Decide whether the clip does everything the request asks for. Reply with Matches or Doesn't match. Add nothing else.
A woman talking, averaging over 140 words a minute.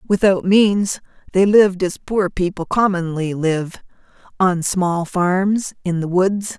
Doesn't match